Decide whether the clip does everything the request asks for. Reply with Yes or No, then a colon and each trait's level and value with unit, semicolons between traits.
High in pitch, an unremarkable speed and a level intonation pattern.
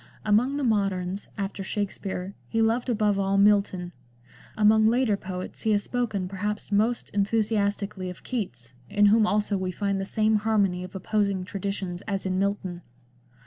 Yes: high, 200 Hz; average, 155 wpm; narrow, 2.1 semitones